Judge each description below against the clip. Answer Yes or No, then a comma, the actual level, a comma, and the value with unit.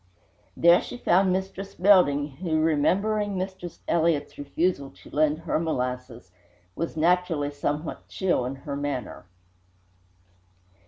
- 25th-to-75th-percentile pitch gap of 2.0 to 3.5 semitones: No, average, 4.2 semitones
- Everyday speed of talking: No, slow, 115 wpm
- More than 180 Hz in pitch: No, medium, 160 Hz